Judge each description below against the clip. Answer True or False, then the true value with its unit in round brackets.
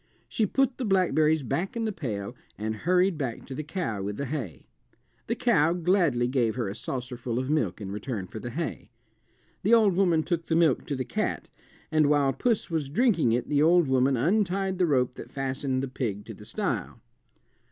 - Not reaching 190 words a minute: False (200 wpm)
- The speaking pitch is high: False (145 Hz)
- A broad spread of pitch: True (6.3 semitones)